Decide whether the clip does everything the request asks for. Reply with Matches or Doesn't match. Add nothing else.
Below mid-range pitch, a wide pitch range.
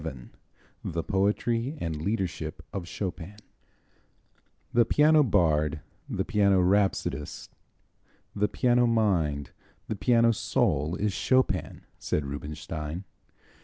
Matches